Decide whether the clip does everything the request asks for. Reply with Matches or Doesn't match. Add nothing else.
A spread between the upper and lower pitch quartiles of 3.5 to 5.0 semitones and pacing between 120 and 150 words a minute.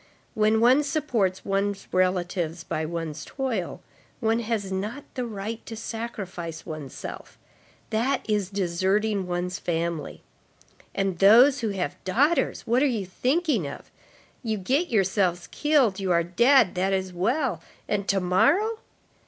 Matches